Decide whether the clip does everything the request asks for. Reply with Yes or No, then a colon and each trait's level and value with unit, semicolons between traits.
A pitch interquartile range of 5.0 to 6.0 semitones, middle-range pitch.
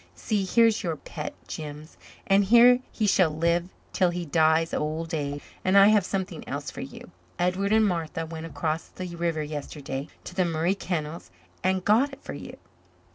No: average, 3.7 semitones; medium, 170 Hz